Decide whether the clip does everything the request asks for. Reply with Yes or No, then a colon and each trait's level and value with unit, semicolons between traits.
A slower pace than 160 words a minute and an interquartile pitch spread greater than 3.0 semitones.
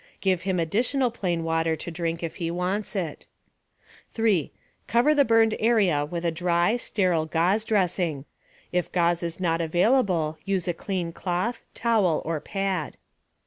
Yes: average, 150 wpm; average, 3.9 semitones